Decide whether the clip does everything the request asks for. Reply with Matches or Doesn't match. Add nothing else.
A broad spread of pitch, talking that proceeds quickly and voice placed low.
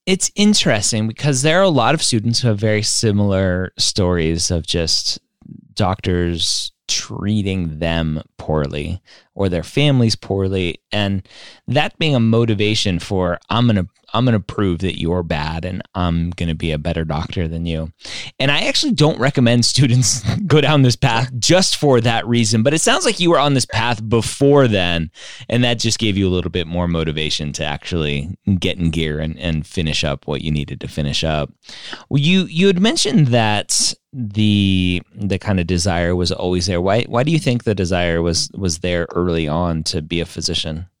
Doesn't match